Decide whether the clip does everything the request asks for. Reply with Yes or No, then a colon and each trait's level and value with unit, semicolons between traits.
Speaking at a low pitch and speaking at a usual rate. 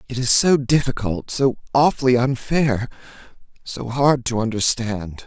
No: low, 125 Hz; slow, 100 wpm